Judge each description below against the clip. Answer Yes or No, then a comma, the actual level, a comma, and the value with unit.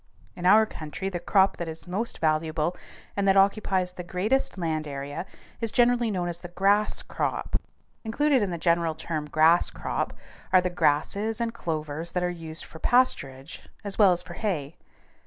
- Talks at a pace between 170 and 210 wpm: Yes, average, 175 wpm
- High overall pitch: No, medium, 180 Hz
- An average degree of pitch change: Yes, average, 4.0 semitones